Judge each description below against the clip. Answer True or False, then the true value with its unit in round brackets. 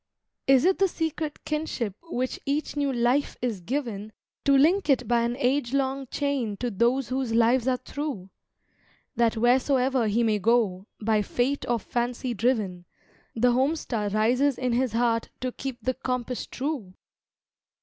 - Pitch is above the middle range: True (250 Hz)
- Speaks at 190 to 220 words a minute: False (160 wpm)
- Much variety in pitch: False (3.0 semitones)